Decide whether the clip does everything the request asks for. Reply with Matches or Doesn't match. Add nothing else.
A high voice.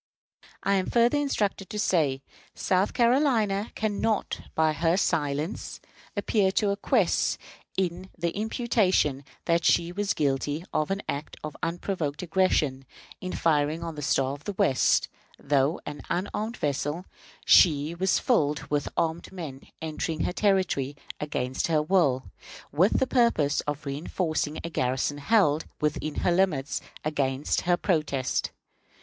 Doesn't match